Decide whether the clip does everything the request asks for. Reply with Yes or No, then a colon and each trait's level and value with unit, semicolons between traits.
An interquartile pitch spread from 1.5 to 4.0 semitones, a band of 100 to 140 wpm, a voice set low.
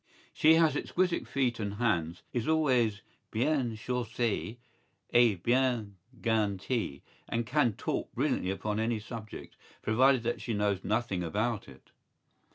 Yes: average, 3.3 semitones; slow, 135 wpm; low, 115 Hz